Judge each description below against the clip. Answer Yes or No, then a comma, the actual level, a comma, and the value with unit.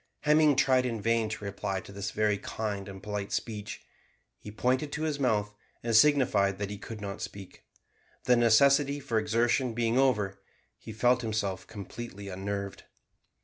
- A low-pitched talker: Yes, low, 110 Hz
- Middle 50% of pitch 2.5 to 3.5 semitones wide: No, average, 3.9 semitones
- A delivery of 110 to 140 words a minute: No, average, 160 wpm